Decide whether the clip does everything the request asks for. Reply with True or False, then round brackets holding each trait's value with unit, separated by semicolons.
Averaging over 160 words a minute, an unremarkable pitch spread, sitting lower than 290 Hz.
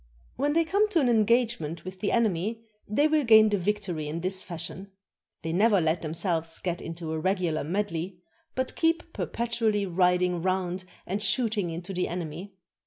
True (175 wpm; 4.5 semitones; 190 Hz)